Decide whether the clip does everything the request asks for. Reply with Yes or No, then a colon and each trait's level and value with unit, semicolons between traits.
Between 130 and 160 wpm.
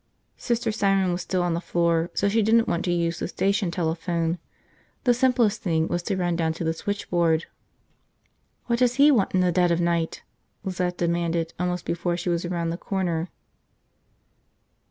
No: average, 175 wpm